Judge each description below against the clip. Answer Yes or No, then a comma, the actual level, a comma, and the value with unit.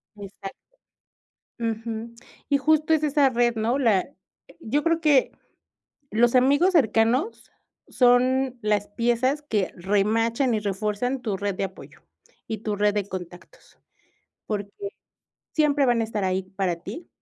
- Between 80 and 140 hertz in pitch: No, high, 230 Hz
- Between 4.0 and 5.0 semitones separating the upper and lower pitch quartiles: Yes, average, 4.7 semitones